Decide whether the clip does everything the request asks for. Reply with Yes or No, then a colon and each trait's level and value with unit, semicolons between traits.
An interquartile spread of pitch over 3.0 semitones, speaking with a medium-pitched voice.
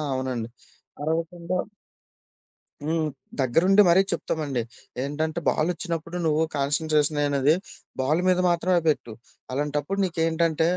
No: narrow, 2.6 semitones; medium, 160 Hz